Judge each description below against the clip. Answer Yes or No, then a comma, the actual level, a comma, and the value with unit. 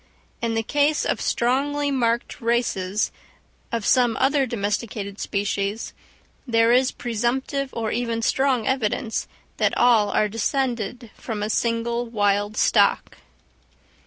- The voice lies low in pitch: No, high, 230 Hz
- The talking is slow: Yes, slow, 120 wpm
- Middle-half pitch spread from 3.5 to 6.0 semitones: No, average, 2.9 semitones